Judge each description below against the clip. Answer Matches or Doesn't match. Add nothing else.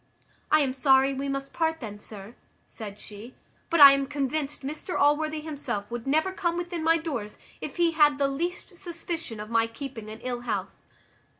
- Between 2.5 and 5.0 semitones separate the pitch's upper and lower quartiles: Doesn't match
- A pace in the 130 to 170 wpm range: Doesn't match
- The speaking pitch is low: Doesn't match